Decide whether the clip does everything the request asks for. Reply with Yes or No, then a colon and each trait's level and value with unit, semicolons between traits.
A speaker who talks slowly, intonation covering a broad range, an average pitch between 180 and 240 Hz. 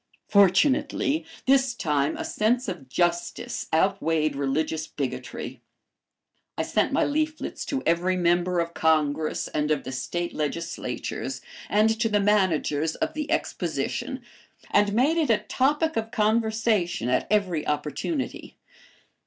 Yes: slow, 130 wpm; wide, 6.1 semitones; medium, 185 Hz